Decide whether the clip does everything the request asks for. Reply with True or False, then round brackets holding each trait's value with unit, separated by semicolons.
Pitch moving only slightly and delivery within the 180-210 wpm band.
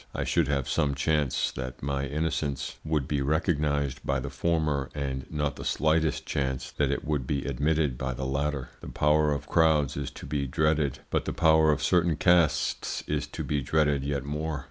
True (2.2 semitones; 190 wpm)